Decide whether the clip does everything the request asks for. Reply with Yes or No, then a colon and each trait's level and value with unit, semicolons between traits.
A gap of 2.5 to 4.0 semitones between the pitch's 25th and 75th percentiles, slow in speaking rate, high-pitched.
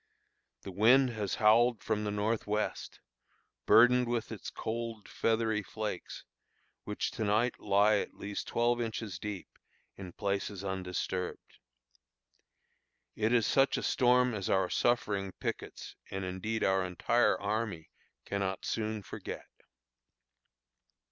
No: average, 2.9 semitones; slow, 120 wpm; low, 105 Hz